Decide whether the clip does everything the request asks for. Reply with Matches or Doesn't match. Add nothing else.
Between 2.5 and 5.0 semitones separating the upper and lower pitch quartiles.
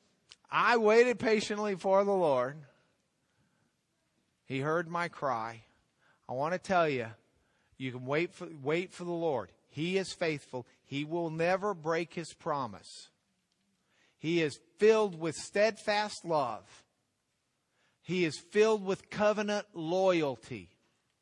Doesn't match